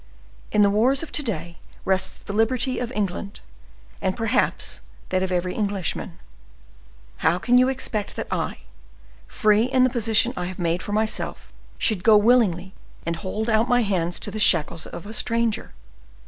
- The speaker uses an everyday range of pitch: Yes, average, 4.1 semitones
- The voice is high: Yes, high, 210 Hz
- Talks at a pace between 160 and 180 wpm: Yes, average, 170 wpm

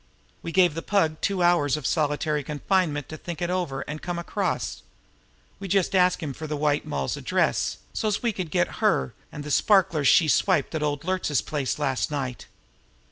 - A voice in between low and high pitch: Yes, medium, 155 Hz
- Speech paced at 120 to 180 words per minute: No, average, 190 wpm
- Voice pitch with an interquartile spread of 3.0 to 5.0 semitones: Yes, average, 3.7 semitones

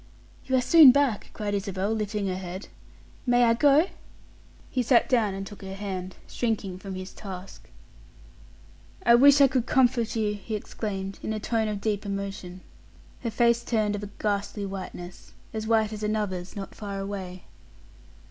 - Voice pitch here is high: Yes, high, 210 Hz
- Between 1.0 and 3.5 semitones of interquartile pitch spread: Yes, average, 3.0 semitones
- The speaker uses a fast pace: No, average, 165 wpm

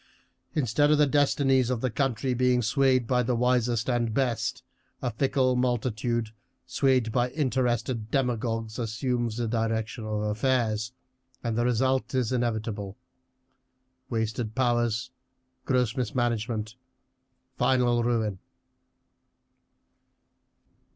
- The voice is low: Yes, low, 120 Hz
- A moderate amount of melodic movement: No, narrow, 2.3 semitones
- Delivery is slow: Yes, slow, 105 wpm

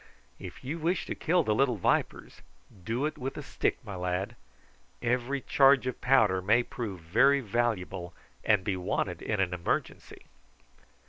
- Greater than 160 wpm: No, average, 155 wpm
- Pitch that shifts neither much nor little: No, wide, 6.4 semitones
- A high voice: No, low, 115 Hz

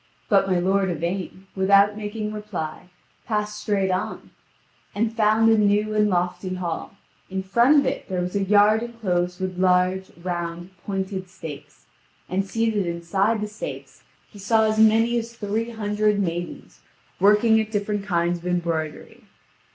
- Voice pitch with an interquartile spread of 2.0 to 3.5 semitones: Yes, average, 2.9 semitones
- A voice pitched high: Yes, high, 200 Hz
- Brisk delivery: No, average, 150 wpm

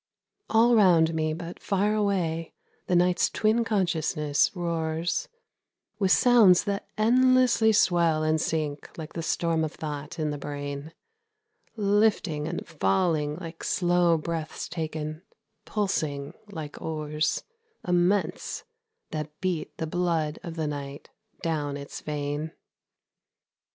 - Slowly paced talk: Yes, slow, 120 wpm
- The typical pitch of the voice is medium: Yes, medium, 165 Hz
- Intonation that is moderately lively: Yes, average, 3.4 semitones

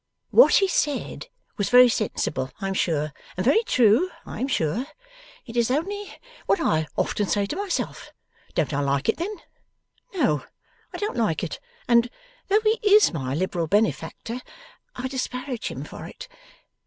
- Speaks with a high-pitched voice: Yes, high, 240 Hz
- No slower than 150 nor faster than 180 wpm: Yes, average, 165 wpm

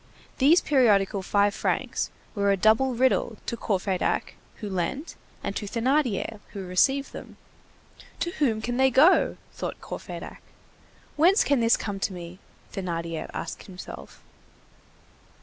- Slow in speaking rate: Yes, slow, 130 wpm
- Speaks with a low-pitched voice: No, high, 215 Hz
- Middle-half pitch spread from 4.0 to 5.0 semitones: No, wide, 5.6 semitones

